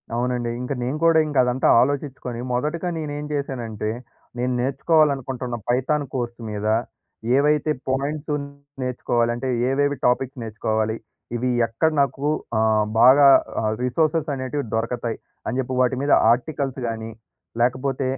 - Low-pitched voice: Yes, low, 130 Hz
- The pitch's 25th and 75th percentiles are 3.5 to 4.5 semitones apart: No, average, 3.0 semitones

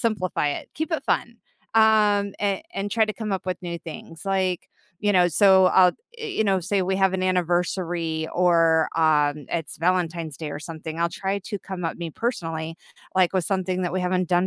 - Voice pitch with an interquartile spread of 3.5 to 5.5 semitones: No, average, 2.8 semitones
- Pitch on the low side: No, medium, 180 Hz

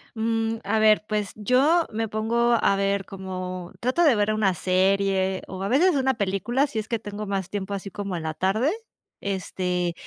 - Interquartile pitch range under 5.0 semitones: Yes, average, 3.0 semitones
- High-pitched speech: Yes, high, 205 Hz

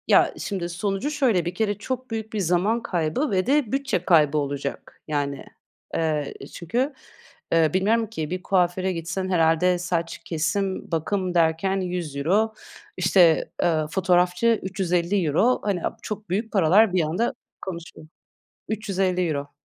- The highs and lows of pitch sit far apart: No, average, 3.8 semitones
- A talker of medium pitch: Yes, medium, 180 Hz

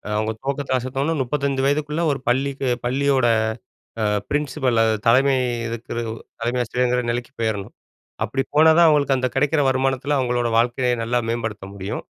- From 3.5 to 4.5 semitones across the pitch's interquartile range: No, average, 2.7 semitones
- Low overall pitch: Yes, low, 130 Hz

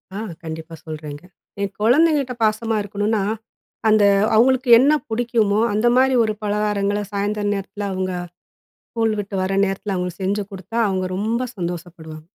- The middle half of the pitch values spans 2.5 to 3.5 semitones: Yes, average, 3.1 semitones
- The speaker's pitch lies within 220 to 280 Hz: No, high, 205 Hz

